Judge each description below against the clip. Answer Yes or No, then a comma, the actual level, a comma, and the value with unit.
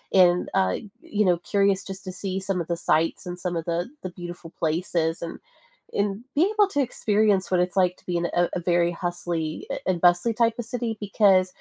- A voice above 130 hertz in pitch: Yes, medium, 185 Hz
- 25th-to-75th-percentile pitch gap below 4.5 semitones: Yes, narrow, 2.6 semitones